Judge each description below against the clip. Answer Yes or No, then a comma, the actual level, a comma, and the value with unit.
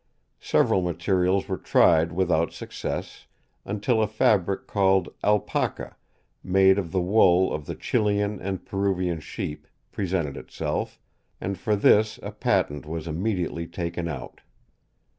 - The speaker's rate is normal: No, slow, 125 wpm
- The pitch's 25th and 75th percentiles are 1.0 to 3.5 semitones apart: Yes, average, 2.9 semitones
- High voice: No, very low, 95 Hz